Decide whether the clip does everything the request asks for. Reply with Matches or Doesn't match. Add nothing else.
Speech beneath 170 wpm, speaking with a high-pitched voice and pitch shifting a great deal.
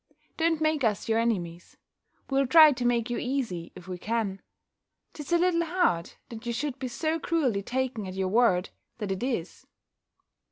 Doesn't match